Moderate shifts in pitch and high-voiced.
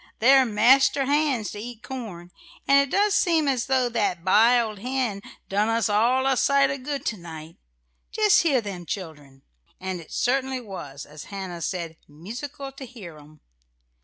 No: wide, 6.6 semitones; high, 230 Hz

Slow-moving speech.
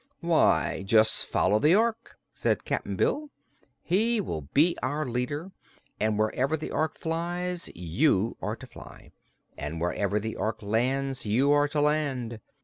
No: average, 145 wpm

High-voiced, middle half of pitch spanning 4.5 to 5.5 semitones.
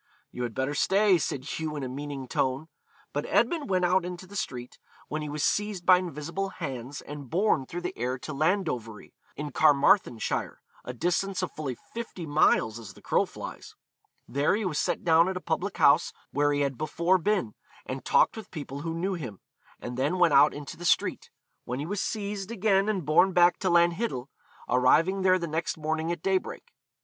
No: medium, 160 Hz; average, 5.0 semitones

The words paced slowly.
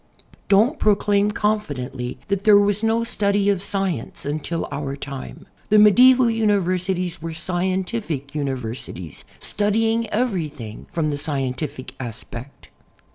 Yes: slow, 120 wpm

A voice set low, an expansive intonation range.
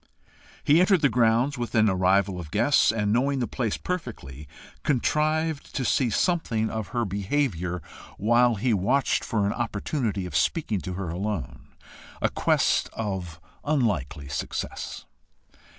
Yes: low, 110 Hz; wide, 5.9 semitones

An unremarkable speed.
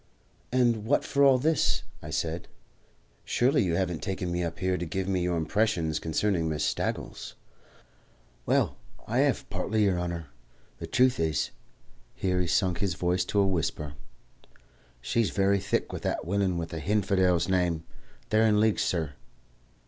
Yes: average, 160 wpm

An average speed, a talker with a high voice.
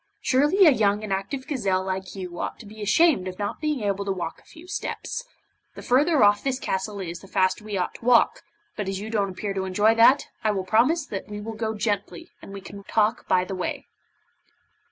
No: fast, 225 wpm; high, 205 Hz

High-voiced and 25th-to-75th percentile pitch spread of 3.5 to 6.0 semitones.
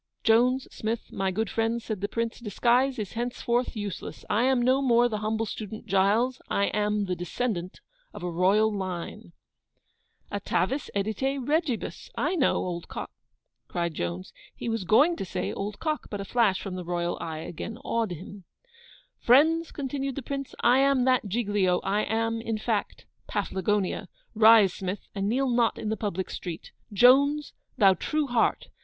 Yes: high, 220 Hz; average, 4.2 semitones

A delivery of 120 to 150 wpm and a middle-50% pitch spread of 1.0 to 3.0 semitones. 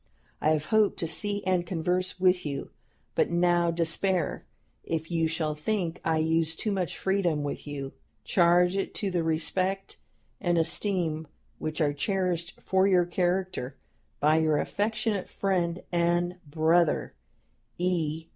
Yes: average, 140 wpm; average, 2.7 semitones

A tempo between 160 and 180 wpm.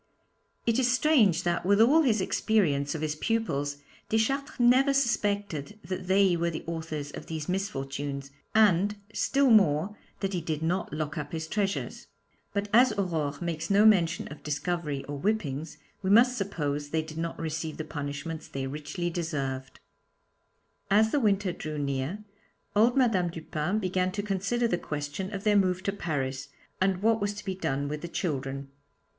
Yes: average, 170 wpm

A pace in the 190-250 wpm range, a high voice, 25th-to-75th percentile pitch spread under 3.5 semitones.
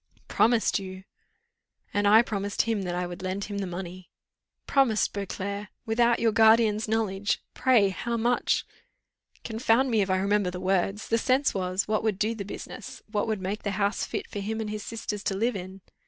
Yes: average, 195 wpm; high, 210 Hz; average, 2.7 semitones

